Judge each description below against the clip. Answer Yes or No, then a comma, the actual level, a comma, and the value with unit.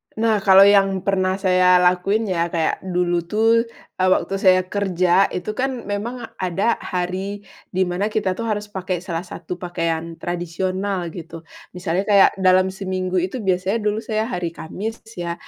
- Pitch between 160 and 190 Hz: Yes, medium, 185 Hz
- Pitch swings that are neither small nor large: No, narrow, 2.3 semitones